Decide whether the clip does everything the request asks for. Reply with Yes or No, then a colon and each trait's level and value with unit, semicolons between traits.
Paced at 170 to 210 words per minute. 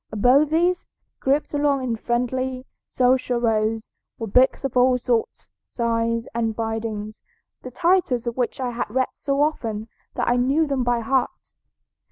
No: average, 155 wpm